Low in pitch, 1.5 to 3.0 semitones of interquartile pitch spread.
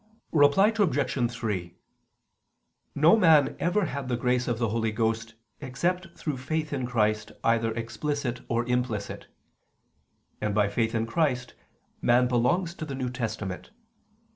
No: low, 125 Hz; average, 4.3 semitones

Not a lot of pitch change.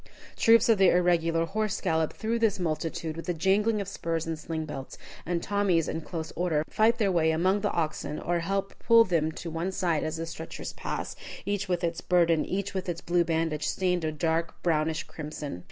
No: average, 3.1 semitones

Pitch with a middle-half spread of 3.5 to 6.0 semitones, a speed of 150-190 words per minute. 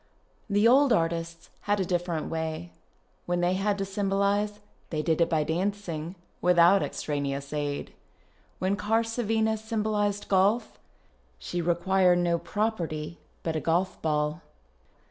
No: average, 3.9 semitones; slow, 135 wpm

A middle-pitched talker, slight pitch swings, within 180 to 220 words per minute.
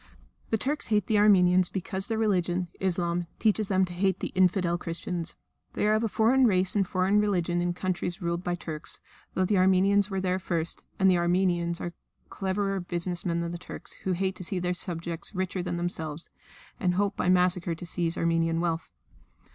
Yes: medium, 180 Hz; narrow, 1.9 semitones; average, 195 wpm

